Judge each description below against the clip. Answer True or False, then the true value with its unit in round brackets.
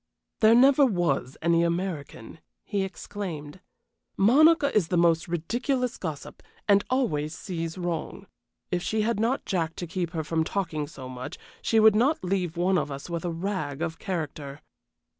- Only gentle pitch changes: False (4.4 semitones)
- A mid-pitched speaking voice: True (175 Hz)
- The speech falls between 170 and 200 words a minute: False (160 wpm)